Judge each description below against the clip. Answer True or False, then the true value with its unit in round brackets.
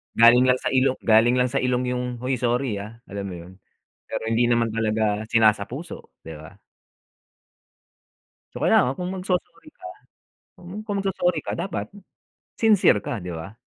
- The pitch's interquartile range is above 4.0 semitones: False (3.5 semitones)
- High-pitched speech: False (120 Hz)